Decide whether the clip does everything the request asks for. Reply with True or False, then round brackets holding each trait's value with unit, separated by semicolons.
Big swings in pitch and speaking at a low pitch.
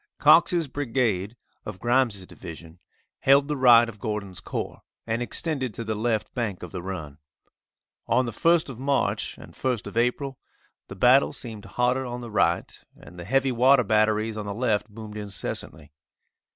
False (4.1 semitones; 115 Hz)